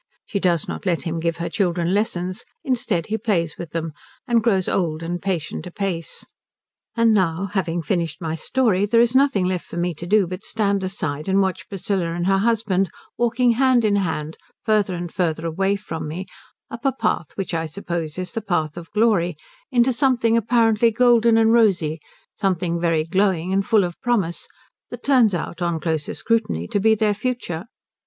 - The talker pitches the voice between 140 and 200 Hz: Yes, high, 190 Hz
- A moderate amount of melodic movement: Yes, average, 4.7 semitones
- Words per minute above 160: Yes, average, 185 wpm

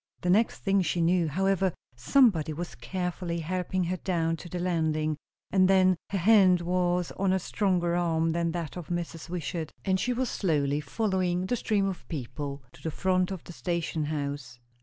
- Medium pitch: Yes, medium, 175 Hz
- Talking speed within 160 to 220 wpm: Yes, average, 180 wpm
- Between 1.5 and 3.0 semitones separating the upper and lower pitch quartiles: Yes, narrow, 2.5 semitones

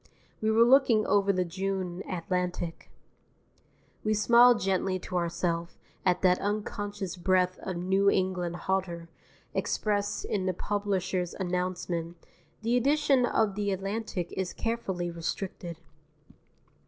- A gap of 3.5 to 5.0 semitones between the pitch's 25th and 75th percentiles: No, narrow, 2.6 semitones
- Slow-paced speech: Yes, slow, 115 wpm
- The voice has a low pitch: No, high, 190 Hz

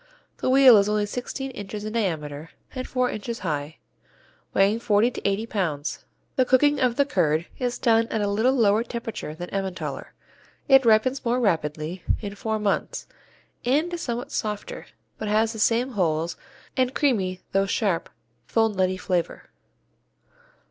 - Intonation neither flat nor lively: Yes, average, 4.8 semitones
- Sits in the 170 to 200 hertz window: No, high, 215 Hz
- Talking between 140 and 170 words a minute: Yes, average, 155 wpm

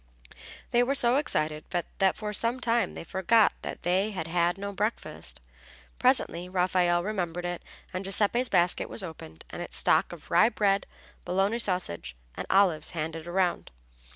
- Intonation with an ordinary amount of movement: Yes, average, 3.6 semitones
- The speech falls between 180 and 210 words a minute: No, average, 155 wpm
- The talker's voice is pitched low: No, high, 190 Hz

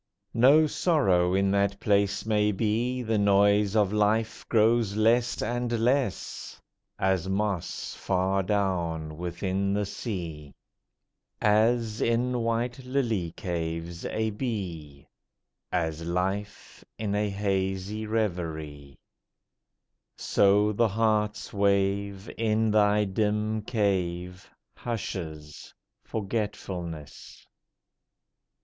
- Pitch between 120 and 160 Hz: No, low, 100 Hz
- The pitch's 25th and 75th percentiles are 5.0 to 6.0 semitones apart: No, average, 3.0 semitones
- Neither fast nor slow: No, slow, 95 wpm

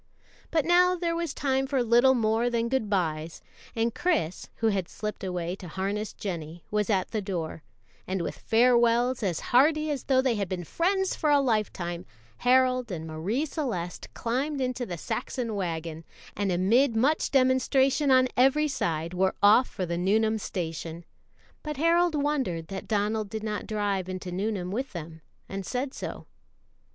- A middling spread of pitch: No, wide, 6.2 semitones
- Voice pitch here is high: Yes, high, 220 Hz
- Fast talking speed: No, average, 165 wpm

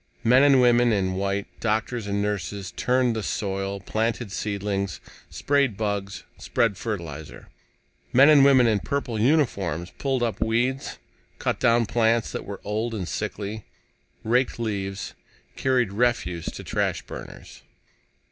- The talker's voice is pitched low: Yes, low, 110 Hz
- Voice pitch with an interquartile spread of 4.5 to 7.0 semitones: No, average, 3.7 semitones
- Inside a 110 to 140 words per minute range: Yes, slow, 135 wpm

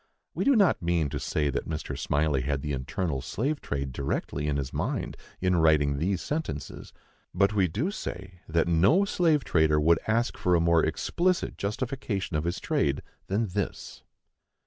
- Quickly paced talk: No, average, 170 wpm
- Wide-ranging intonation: Yes, wide, 6.0 semitones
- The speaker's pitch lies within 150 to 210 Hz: No, very low, 85 Hz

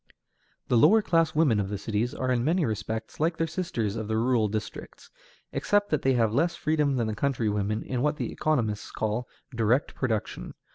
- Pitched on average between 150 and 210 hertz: No, low, 120 Hz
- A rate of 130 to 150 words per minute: No, average, 195 wpm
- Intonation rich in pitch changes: Yes, wide, 5.7 semitones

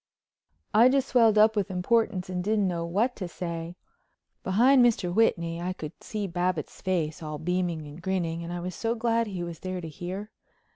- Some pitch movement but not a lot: Yes, average, 4.1 semitones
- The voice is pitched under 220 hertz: Yes, medium, 185 Hz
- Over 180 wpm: Yes, average, 190 wpm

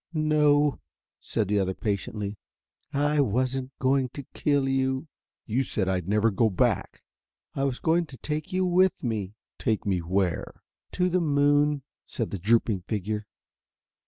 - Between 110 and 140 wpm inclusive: No, average, 150 wpm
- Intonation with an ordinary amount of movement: No, wide, 5.9 semitones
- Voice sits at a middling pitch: No, low, 130 Hz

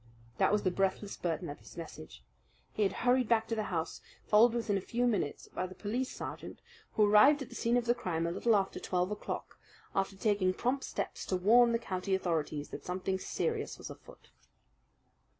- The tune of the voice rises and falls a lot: No, average, 4.3 semitones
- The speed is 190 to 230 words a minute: Yes, average, 200 wpm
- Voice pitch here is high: Yes, high, 205 Hz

